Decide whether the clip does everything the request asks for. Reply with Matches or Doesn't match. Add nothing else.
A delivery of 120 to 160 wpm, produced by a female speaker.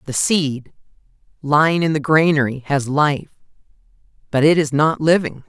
Matches